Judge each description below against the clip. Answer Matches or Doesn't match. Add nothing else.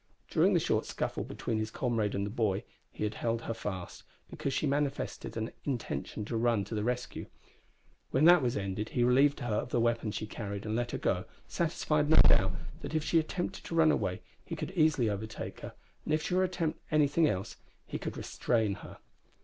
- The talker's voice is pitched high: Doesn't match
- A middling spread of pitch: Doesn't match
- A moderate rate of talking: Doesn't match